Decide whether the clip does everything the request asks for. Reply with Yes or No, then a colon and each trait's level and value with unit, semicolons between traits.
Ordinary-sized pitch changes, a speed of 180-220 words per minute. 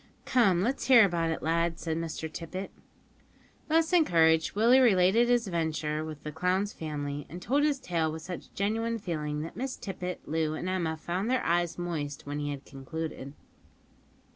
No: average, 4.6 semitones; average, 170 wpm